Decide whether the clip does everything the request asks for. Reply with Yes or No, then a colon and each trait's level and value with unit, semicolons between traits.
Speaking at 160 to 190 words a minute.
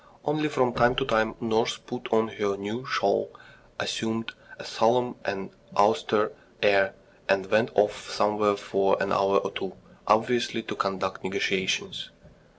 No: average, 145 wpm